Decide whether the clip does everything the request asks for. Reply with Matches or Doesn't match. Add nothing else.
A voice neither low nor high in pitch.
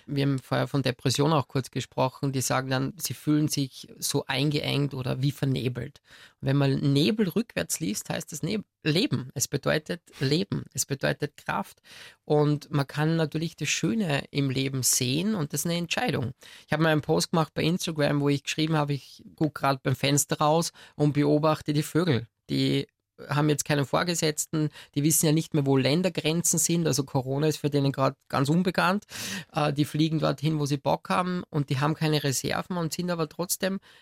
Matches